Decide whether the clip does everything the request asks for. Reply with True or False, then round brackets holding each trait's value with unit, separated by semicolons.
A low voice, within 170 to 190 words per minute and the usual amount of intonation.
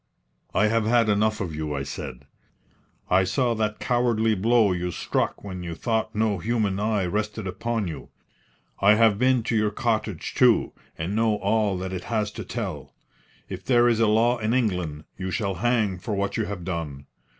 True (105 Hz; 185 wpm; 3.4 semitones)